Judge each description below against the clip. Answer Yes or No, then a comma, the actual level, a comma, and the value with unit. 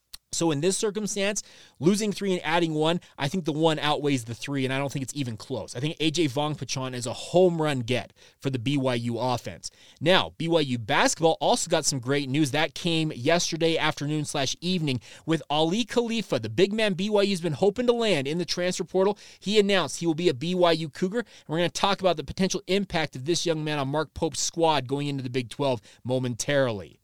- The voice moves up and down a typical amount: Yes, average, 4.5 semitones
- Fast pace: Yes, fast, 215 wpm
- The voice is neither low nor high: Yes, medium, 160 Hz